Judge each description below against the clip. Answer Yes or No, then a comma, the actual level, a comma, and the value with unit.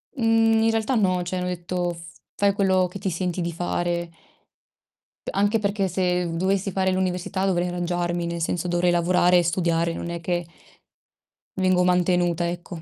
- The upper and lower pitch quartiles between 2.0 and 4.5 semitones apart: No, narrow, 1.5 semitones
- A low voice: No, medium, 180 Hz